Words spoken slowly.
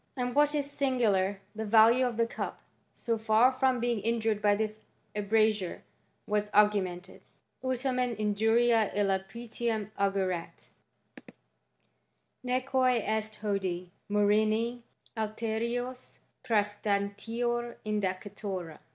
Yes: slow, 105 wpm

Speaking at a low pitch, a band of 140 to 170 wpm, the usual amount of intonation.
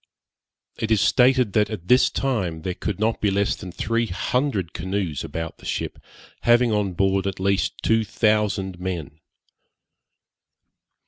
Yes: low, 100 Hz; average, 145 wpm; average, 3.5 semitones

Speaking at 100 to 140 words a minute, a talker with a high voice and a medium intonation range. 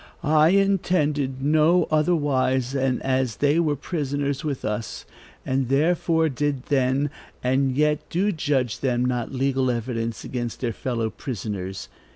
No: slow, 135 wpm; low, 135 Hz; average, 3.1 semitones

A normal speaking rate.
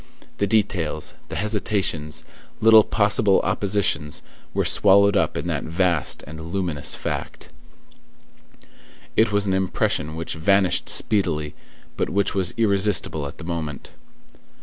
No: slow, 125 wpm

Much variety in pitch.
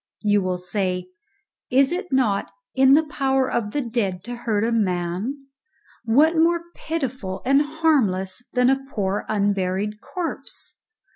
Yes: wide, 5.8 semitones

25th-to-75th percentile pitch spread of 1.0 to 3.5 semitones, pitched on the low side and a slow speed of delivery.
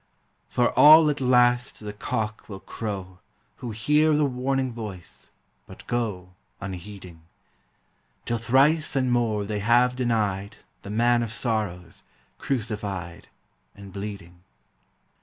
No: average, 3.9 semitones; low, 110 Hz; slow, 120 wpm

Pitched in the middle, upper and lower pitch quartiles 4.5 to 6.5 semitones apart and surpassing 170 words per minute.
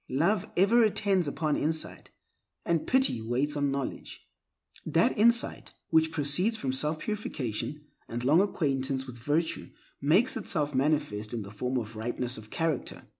No: medium, 145 Hz; average, 5.2 semitones; average, 145 wpm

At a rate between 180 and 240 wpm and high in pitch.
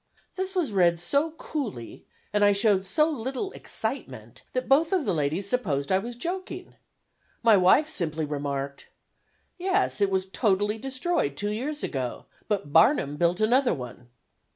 No: average, 155 wpm; high, 205 Hz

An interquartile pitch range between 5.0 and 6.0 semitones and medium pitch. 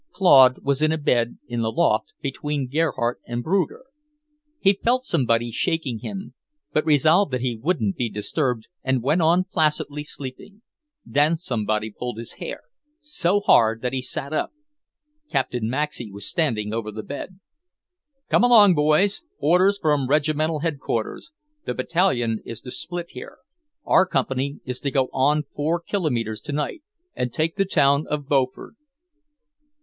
Yes: average, 5.3 semitones; medium, 145 Hz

